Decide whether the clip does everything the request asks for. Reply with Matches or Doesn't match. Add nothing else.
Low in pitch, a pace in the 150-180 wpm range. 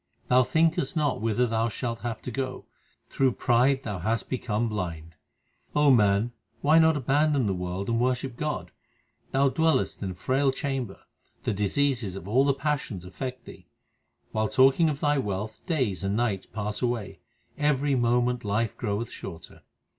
Matches